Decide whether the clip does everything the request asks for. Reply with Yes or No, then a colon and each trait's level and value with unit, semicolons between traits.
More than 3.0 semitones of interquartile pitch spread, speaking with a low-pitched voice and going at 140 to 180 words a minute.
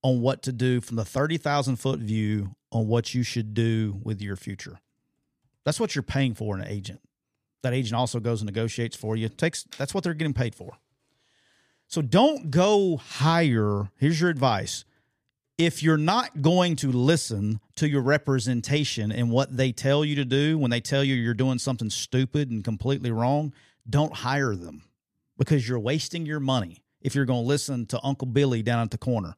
No: average, 4.0 semitones; low, 130 Hz; average, 190 wpm